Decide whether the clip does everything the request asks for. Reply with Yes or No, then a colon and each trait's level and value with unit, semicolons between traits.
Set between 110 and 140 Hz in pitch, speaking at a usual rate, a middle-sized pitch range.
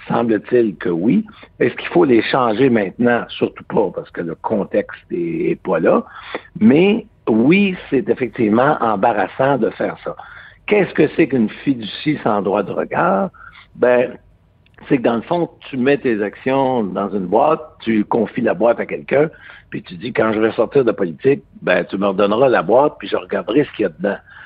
No: low, 135 Hz; average, 190 wpm; wide, 7.0 semitones